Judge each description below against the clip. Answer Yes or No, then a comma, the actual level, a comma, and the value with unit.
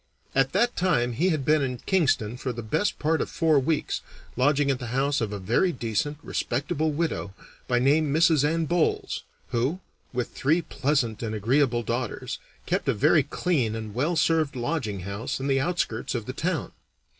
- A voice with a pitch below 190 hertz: Yes, low, 135 Hz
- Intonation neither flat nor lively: Yes, average, 4.8 semitones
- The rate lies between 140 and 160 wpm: No, average, 180 wpm